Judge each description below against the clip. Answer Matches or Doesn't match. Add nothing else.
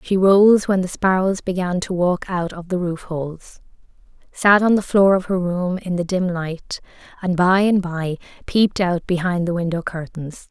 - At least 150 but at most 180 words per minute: Doesn't match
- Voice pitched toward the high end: Doesn't match